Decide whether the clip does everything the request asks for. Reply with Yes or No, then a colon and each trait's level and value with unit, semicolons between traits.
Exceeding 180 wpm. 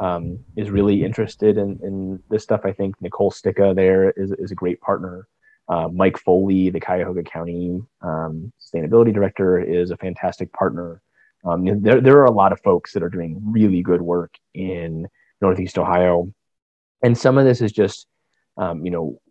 No: average, 175 wpm